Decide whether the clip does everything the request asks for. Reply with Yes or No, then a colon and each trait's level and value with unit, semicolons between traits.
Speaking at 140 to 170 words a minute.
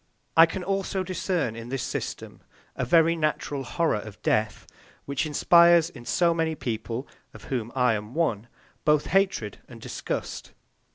Yes: average, 155 wpm